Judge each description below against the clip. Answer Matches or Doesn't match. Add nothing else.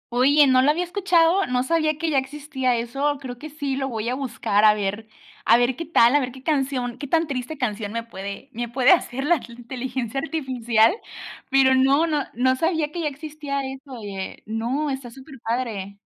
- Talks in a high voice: Matches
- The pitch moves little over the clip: Doesn't match